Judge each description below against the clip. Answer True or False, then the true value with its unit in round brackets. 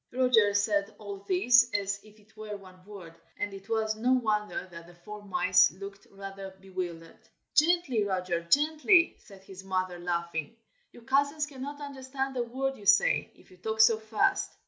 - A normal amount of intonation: True (4.7 semitones)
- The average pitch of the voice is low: False (210 Hz)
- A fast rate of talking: False (170 wpm)